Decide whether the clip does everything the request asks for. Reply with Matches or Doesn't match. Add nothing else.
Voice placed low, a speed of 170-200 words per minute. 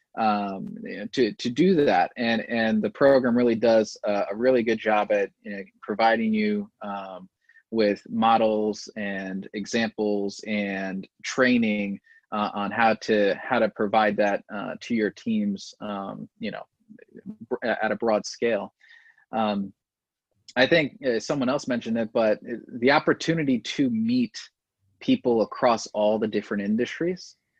Doesn't match